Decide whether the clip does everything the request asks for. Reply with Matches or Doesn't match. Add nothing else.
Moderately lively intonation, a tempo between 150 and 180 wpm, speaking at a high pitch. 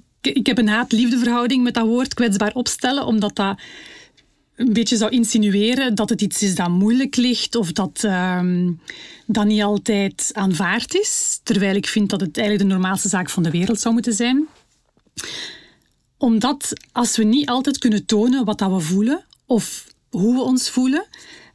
Matches